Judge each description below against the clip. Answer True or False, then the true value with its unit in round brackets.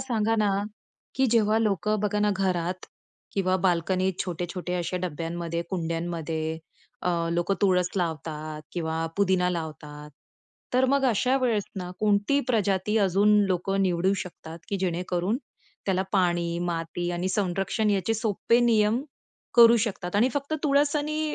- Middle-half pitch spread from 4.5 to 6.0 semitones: False (3.6 semitones)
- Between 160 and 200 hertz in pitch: True (190 Hz)